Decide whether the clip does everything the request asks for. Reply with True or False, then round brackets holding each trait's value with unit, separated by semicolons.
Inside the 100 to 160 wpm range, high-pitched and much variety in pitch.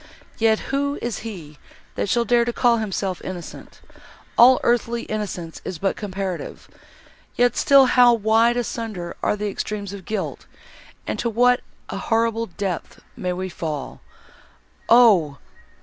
False (135 wpm; 220 Hz; 4.1 semitones)